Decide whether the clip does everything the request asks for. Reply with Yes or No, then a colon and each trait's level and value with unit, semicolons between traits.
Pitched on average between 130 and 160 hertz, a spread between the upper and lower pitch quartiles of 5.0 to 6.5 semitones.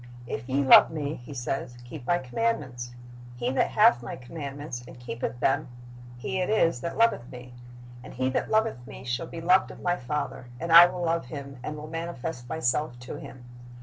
Yes: medium, 140 Hz; average, 5.3 semitones